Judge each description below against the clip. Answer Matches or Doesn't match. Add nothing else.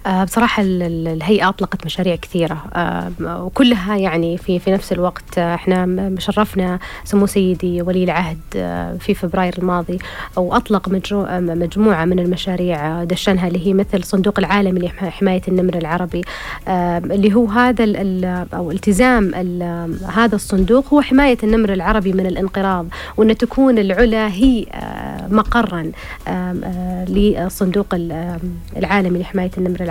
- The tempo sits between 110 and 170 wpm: Matches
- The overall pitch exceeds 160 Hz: Matches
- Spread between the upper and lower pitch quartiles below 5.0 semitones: Matches